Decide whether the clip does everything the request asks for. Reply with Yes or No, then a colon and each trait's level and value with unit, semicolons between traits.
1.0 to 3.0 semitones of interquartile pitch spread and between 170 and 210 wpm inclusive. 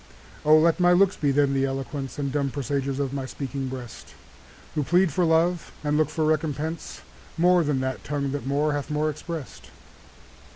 Yes: narrow, 2.6 semitones; average, 190 wpm